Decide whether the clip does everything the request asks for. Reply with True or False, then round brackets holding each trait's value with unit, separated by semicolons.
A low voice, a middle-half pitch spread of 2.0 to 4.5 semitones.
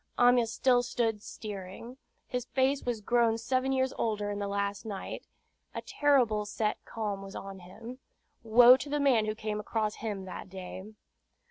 False (225 Hz; 3.3 semitones)